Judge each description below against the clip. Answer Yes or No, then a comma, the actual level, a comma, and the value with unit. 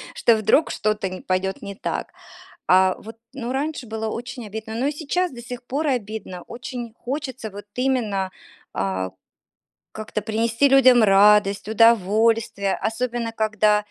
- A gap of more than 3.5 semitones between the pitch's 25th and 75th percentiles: No, average, 3.2 semitones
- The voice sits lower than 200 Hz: No, high, 225 Hz